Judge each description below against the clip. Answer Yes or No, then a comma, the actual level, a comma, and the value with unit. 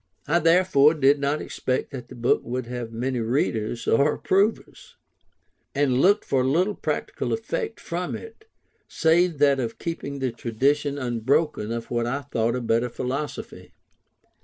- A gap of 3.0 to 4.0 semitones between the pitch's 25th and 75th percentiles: No, average, 4.5 semitones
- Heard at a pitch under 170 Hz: Yes, low, 135 Hz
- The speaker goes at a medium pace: Yes, average, 150 wpm